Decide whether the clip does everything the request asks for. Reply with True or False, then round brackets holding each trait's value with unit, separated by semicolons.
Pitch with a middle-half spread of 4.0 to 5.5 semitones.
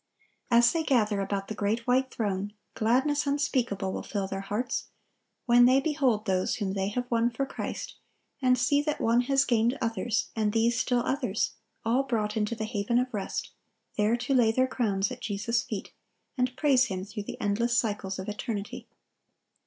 False (3.4 semitones)